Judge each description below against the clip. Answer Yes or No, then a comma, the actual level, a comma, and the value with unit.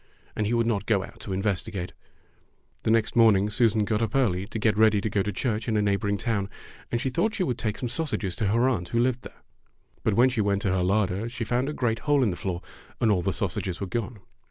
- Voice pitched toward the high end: No, low, 110 Hz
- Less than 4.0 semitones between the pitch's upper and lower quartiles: Yes, average, 3.0 semitones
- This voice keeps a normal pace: No, fast, 255 wpm